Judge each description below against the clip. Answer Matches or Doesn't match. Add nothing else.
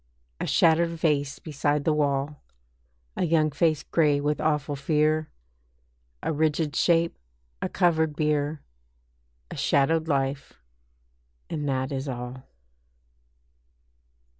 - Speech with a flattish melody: Matches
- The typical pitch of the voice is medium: Matches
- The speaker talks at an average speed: Doesn't match